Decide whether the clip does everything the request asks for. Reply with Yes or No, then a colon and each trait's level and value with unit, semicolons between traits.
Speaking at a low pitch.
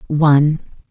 No: medium, 145 Hz